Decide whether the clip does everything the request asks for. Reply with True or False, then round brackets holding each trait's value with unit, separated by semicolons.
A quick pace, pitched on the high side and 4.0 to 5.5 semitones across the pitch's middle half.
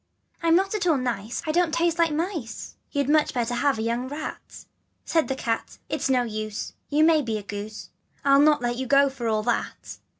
True (225 wpm; 270 Hz; 5.1 semitones)